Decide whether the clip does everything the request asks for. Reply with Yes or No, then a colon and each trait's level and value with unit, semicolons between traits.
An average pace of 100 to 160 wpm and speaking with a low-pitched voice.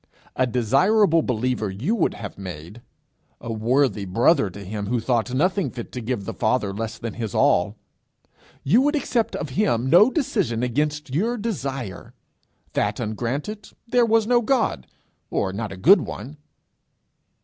Yes: average, 155 wpm; low, 125 Hz